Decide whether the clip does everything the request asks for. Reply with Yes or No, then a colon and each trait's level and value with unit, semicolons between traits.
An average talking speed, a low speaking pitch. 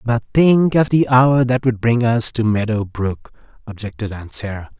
Yes: average, 190 wpm; low, 115 Hz